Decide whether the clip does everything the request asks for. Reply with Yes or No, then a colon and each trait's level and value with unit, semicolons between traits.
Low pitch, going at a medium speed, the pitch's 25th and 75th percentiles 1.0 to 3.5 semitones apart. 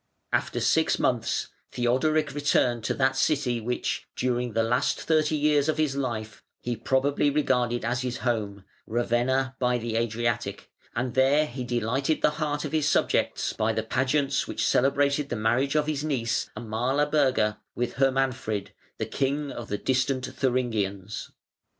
Yes: low, 130 Hz; average, 150 wpm; average, 3.2 semitones